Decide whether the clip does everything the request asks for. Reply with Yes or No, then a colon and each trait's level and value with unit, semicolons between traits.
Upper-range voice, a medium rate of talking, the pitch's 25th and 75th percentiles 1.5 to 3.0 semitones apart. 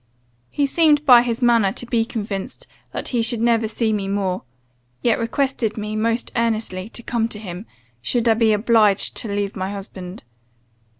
Yes: high, 225 Hz; average, 175 wpm; average, 2.7 semitones